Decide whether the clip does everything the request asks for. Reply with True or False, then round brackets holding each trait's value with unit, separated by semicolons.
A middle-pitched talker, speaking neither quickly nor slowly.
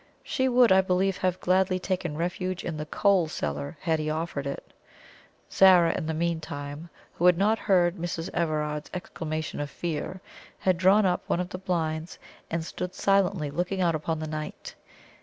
True (170 Hz; 175 wpm)